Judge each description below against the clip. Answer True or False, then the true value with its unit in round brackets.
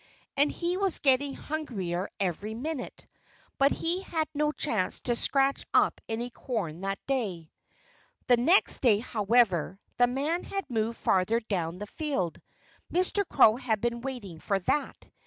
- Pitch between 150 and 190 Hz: False (240 Hz)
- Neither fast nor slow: True (150 wpm)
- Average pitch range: False (6.4 semitones)